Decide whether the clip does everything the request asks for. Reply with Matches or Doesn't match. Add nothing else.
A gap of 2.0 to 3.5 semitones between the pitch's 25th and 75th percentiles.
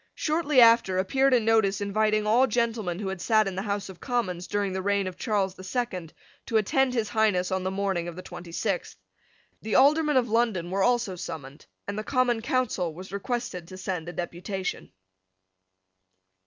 Doesn't match